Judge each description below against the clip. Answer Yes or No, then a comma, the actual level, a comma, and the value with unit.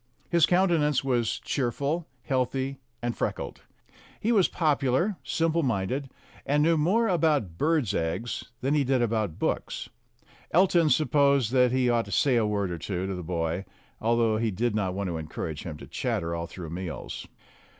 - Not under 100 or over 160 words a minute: No, average, 170 wpm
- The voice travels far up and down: Yes, wide, 7.4 semitones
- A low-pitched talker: Yes, low, 125 Hz